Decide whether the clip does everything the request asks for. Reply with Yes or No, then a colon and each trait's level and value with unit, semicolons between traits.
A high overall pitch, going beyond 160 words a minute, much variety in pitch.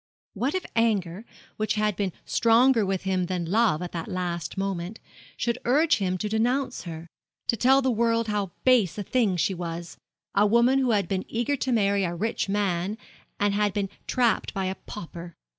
No: high, 205 Hz; average, 190 wpm; average, 4.1 semitones